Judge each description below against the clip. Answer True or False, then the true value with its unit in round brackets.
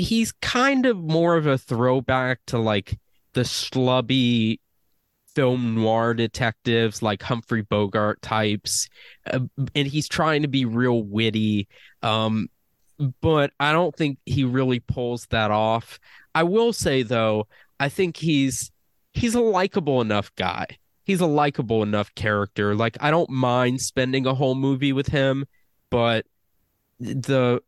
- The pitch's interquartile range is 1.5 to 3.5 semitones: False (4.2 semitones)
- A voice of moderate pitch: False (125 Hz)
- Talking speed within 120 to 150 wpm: True (140 wpm)